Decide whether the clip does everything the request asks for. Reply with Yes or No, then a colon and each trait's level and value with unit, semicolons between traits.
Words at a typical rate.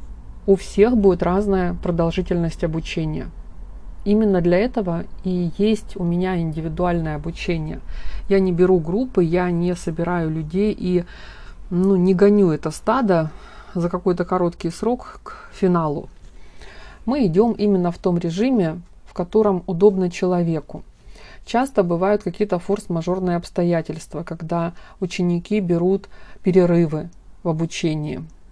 Yes: average, 120 wpm